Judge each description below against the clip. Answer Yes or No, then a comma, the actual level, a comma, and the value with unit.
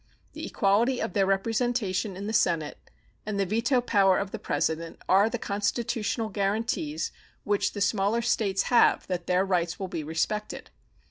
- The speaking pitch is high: Yes, high, 200 Hz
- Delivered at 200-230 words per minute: No, average, 160 wpm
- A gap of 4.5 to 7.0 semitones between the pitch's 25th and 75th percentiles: No, average, 3.1 semitones